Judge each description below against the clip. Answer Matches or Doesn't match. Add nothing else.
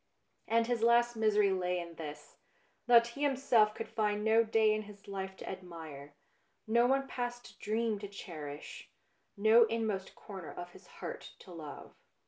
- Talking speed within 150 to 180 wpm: Matches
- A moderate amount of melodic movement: Matches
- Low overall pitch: Doesn't match